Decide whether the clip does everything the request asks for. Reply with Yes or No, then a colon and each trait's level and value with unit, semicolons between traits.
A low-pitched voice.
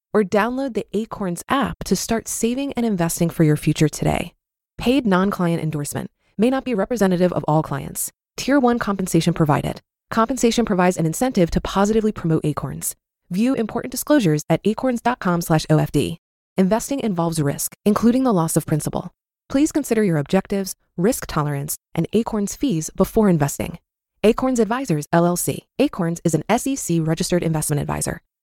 No: medium, 185 Hz